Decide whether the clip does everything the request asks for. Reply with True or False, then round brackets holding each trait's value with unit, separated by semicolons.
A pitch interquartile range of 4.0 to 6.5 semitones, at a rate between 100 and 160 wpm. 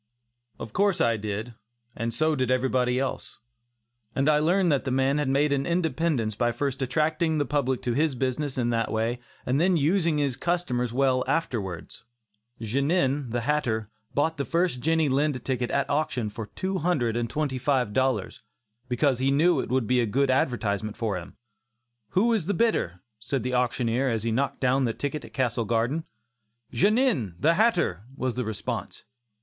False (4.4 semitones; 180 wpm)